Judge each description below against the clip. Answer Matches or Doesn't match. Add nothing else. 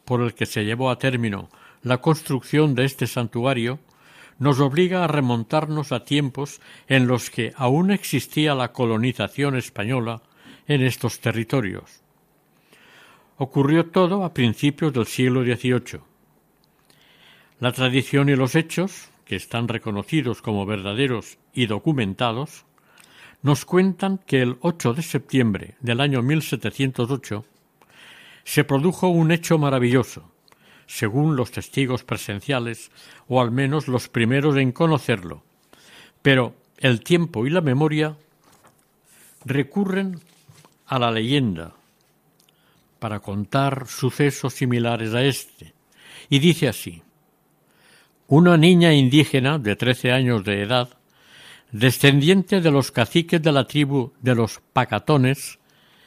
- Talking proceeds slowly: Matches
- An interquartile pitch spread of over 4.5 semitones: Doesn't match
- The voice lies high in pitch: Doesn't match